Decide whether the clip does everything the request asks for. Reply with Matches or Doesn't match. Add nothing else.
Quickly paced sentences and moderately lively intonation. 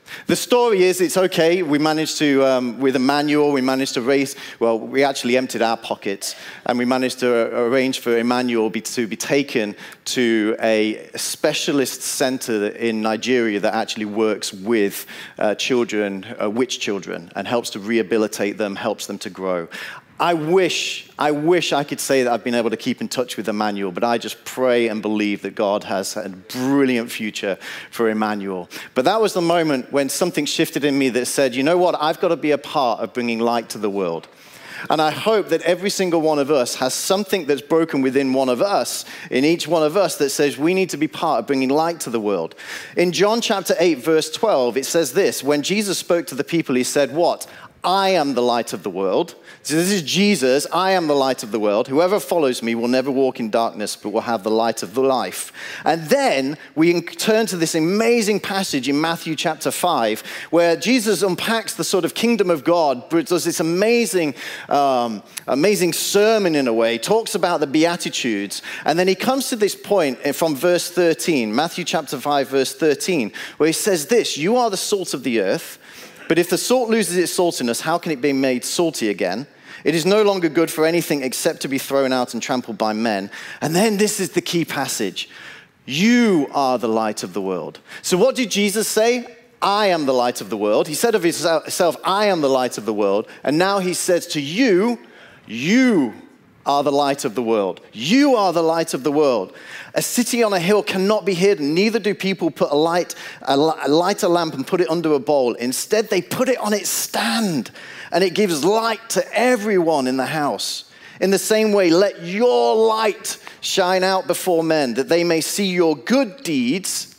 Doesn't match